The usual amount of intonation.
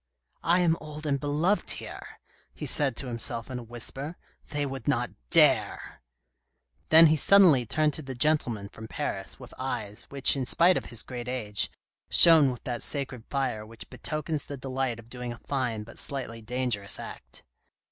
Yes: average, 4.3 semitones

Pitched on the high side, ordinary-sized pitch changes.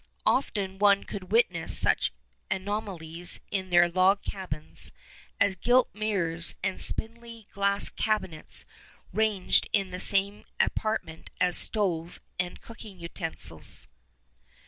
Yes: high, 195 Hz; average, 3.3 semitones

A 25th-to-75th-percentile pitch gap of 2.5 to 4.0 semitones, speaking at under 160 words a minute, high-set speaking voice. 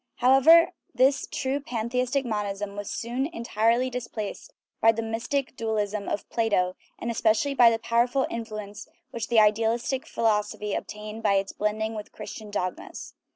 Yes: average, 3.0 semitones; average, 150 wpm; high, 225 Hz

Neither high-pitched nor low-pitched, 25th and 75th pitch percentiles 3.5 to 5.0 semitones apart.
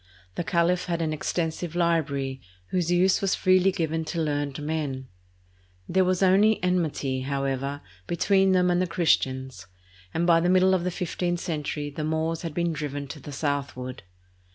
Yes: medium, 165 Hz; average, 3.9 semitones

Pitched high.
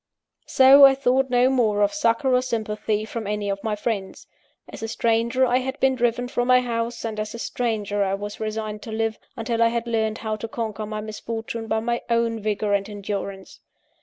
Yes: high, 225 Hz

